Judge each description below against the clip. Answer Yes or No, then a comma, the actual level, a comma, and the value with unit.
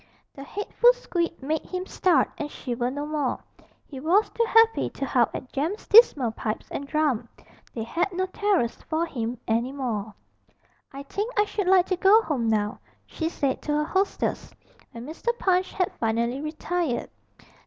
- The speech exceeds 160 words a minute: Yes, average, 170 wpm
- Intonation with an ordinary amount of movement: No, wide, 7.0 semitones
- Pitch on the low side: No, very high, 305 Hz